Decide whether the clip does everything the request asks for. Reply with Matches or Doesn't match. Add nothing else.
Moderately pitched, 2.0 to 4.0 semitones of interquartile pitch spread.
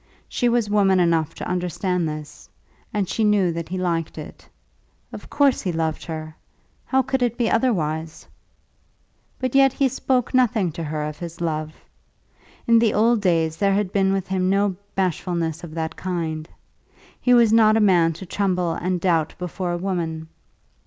Doesn't match